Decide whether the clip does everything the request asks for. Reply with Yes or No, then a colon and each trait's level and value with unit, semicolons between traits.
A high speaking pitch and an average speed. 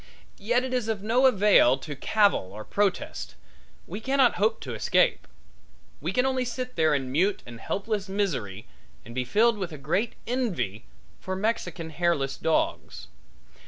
Yes: high, 195 Hz; average, 160 wpm